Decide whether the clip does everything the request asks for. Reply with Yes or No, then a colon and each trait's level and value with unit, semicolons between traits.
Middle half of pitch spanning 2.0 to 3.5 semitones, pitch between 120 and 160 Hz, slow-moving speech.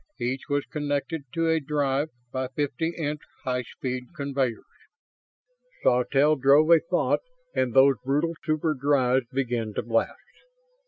Yes: average, 2.9 semitones; medium, 140 Hz; slow, 130 wpm